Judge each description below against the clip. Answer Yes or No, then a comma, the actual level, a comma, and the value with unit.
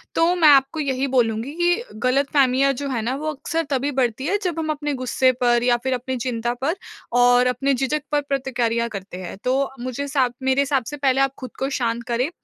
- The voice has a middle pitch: No, very high, 265 Hz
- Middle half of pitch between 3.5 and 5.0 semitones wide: No, narrow, 2.5 semitones